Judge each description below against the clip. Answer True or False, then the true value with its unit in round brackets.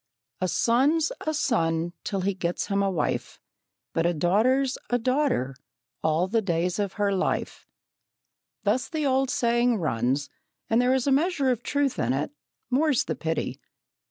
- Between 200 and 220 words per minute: False (160 wpm)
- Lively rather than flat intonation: True (7.3 semitones)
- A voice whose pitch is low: False (220 Hz)